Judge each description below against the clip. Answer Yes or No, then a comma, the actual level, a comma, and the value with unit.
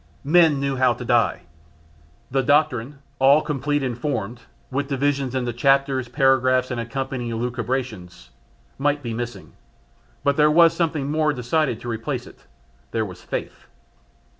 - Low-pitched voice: Yes, low, 130 Hz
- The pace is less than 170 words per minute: Yes, average, 140 wpm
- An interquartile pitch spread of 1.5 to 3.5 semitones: Yes, average, 3.0 semitones